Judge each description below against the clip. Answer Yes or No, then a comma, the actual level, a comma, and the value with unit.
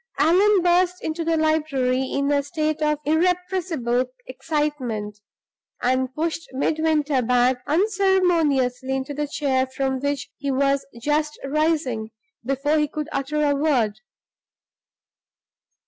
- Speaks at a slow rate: Yes, slow, 115 wpm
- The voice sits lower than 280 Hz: No, very high, 290 Hz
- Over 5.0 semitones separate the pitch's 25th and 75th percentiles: No, average, 3.3 semitones